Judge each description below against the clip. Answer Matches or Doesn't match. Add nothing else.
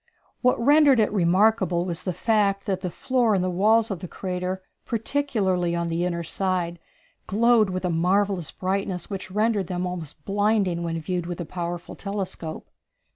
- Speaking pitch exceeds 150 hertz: Matches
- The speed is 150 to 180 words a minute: Matches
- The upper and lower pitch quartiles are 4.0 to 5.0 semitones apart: Doesn't match